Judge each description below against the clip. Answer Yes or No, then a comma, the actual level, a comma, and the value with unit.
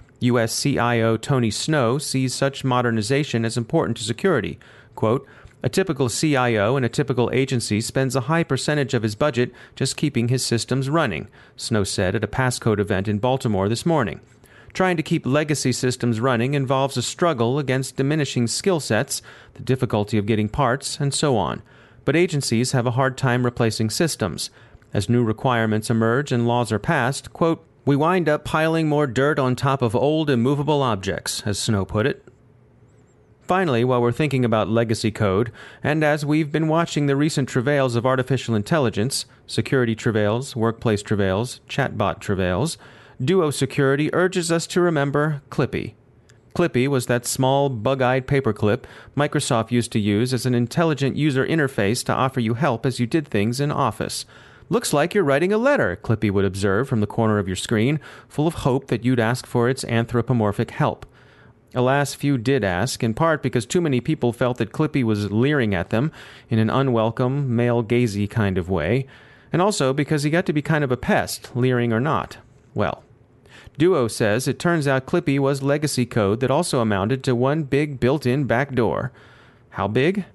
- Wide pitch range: No, average, 3.9 semitones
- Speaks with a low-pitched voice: Yes, low, 125 Hz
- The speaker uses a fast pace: No, average, 180 wpm